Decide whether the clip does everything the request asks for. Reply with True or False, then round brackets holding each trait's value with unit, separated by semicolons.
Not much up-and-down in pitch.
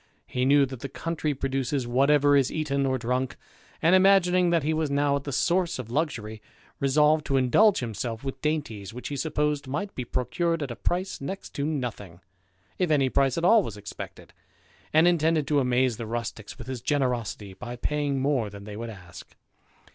False (4.1 semitones)